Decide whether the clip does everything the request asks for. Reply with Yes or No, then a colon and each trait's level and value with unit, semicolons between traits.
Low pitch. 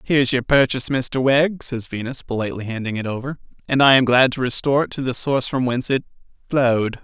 Yes: low, 130 Hz